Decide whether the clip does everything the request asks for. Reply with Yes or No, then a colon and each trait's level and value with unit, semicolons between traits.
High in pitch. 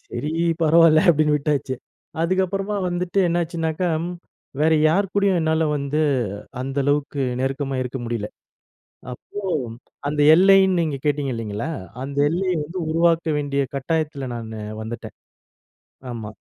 No: medium, 155 Hz